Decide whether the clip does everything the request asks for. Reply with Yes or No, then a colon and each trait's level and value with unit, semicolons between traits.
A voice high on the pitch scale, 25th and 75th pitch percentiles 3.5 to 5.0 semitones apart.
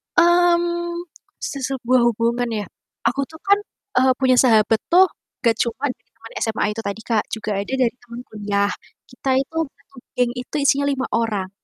Yes: high, 245 Hz; average, 4.0 semitones